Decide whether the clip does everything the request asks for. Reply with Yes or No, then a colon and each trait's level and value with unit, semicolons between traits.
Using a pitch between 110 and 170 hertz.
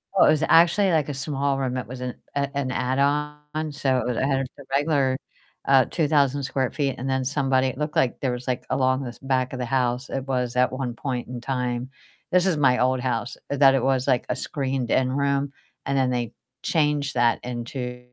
Yes: low, 135 Hz